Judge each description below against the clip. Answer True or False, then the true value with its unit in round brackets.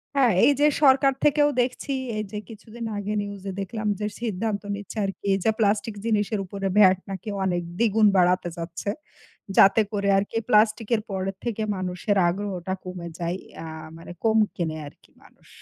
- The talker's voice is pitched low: False (205 Hz)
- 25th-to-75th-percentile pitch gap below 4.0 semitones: True (3.1 semitones)